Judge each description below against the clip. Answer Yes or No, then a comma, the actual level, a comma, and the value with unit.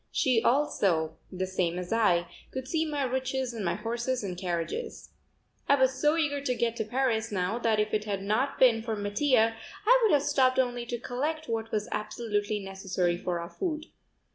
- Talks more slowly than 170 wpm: No, average, 190 wpm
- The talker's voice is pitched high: Yes, high, 230 Hz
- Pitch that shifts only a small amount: No, average, 4.5 semitones